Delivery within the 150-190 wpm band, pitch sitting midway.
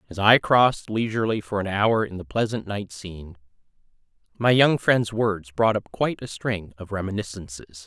No: average, 175 wpm; low, 105 Hz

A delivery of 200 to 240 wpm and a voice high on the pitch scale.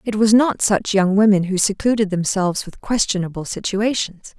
No: average, 165 wpm; high, 200 Hz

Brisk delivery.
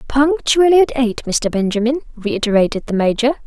No: average, 140 wpm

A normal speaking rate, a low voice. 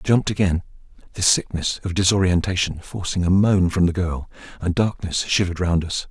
Yes: average, 175 wpm; very low, 90 Hz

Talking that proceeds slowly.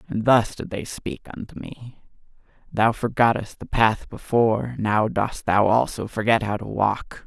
No: average, 165 wpm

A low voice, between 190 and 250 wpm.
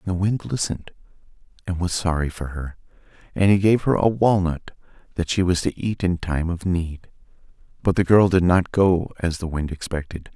Yes: very low, 90 Hz; average, 195 wpm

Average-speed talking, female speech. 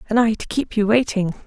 No: fast, 245 wpm; female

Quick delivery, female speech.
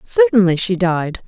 No: average, 140 wpm; female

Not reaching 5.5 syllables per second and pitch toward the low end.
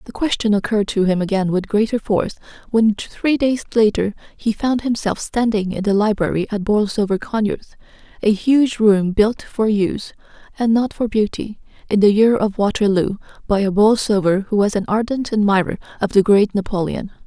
No: 5.2 syllables/s; high, 210 Hz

